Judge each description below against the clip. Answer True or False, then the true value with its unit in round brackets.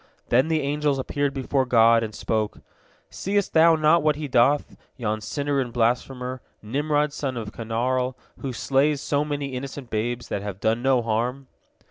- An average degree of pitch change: True (3.7 semitones)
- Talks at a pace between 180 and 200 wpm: False (165 wpm)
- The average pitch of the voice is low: True (130 Hz)